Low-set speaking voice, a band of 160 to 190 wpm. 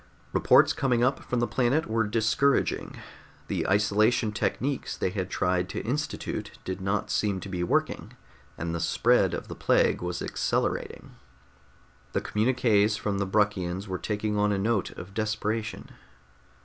No: low, 105 Hz; average, 150 wpm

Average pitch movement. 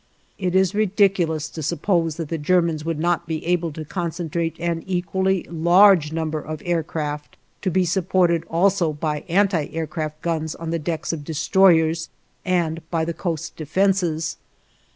No: narrow, 2.3 semitones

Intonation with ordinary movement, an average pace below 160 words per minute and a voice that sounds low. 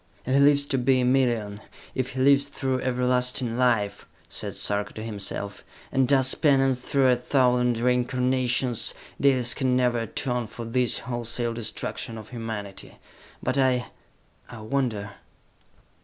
No: narrow, 2.2 semitones; average, 140 wpm; low, 125 Hz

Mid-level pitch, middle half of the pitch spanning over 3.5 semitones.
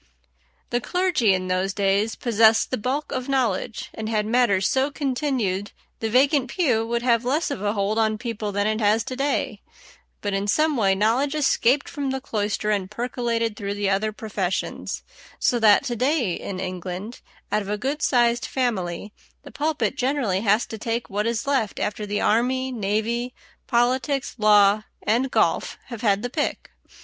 No: high, 225 Hz; average, 3.9 semitones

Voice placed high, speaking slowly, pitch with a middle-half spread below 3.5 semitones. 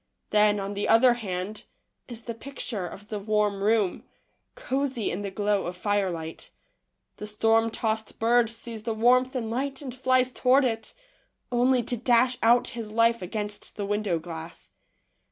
No: high, 225 Hz; average, 165 wpm; average, 2.9 semitones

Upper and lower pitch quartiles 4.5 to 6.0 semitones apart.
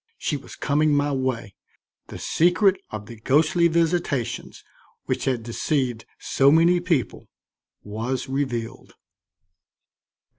Yes: average, 5.2 semitones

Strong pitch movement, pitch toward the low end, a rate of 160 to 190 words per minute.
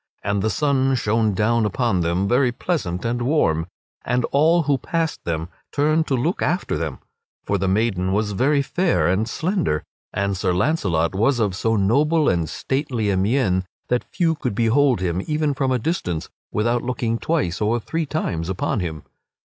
Yes: wide, 7.0 semitones; low, 115 Hz; average, 175 wpm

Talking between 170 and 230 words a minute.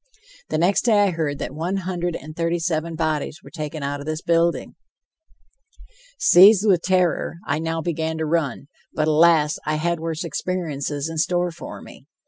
Yes: average, 175 wpm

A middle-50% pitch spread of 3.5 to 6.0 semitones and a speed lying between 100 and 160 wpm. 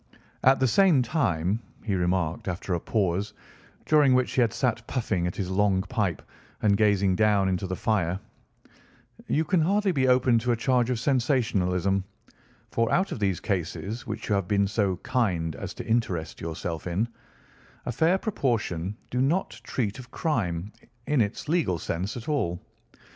No: wide, 5.5 semitones; average, 170 wpm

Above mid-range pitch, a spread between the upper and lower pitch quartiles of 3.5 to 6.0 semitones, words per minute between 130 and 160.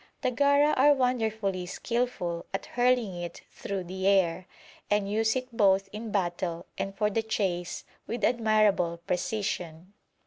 Yes: high, 205 Hz; average, 4.3 semitones; average, 140 wpm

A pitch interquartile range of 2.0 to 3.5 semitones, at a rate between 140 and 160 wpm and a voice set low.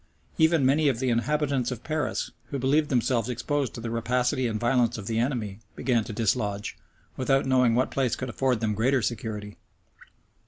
No: average, 2.9 semitones; average, 175 wpm; low, 125 Hz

